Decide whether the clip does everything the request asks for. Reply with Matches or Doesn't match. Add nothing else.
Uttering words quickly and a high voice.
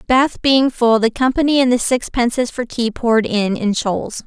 Doesn't match